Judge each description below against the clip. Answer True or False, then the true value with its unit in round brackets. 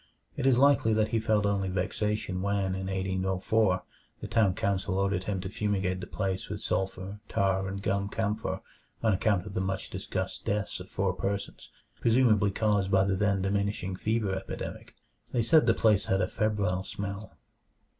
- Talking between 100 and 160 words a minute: False (175 wpm)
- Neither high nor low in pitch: False (100 Hz)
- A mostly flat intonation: True (2.0 semitones)